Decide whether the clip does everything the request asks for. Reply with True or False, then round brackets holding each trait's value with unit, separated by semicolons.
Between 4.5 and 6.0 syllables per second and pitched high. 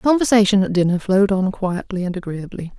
False (6.3 syllables/s; 195 Hz)